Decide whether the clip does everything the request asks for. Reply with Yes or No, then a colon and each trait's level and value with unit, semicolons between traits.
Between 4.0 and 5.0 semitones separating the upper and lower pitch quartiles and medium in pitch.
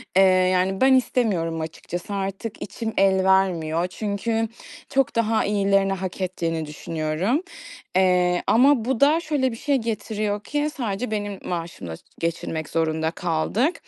No: average, 4.6 semitones; high, 195 Hz